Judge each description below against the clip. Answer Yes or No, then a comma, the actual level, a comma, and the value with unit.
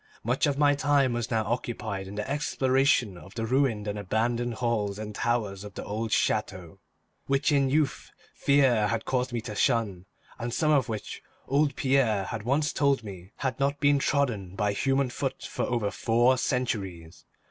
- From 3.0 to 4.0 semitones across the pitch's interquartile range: No, average, 4.6 semitones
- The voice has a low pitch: Yes, low, 120 Hz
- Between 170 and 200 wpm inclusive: Yes, average, 180 wpm